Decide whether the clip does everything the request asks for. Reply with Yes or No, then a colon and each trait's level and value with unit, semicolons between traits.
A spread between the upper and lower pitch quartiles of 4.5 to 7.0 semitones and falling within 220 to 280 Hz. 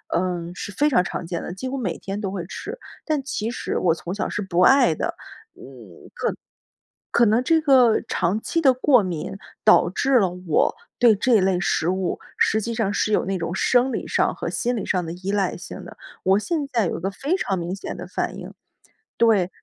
No: wide, 5.4 semitones; high, 200 Hz